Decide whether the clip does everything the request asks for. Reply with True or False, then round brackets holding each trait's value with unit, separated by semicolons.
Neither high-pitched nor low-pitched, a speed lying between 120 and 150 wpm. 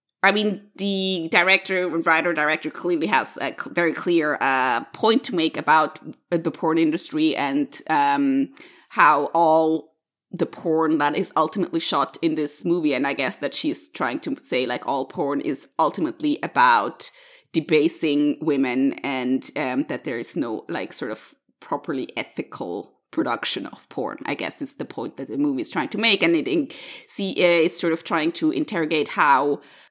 False (175 Hz; 170 wpm)